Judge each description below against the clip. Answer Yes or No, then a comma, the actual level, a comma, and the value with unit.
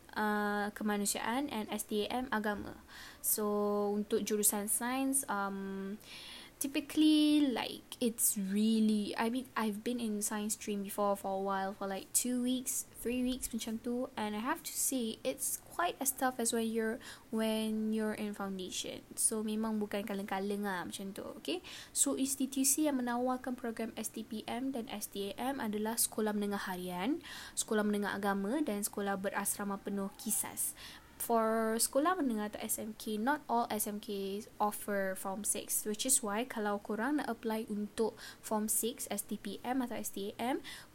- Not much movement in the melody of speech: No, average, 3.3 semitones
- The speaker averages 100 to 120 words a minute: No, average, 150 wpm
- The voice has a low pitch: No, high, 220 Hz